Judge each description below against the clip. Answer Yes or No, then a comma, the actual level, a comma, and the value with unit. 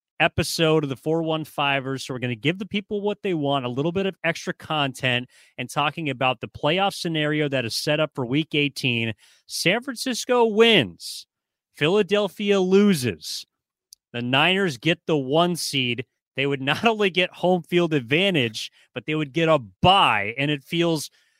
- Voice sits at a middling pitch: Yes, medium, 155 Hz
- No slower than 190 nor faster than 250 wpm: No, average, 170 wpm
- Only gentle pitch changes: No, average, 5.1 semitones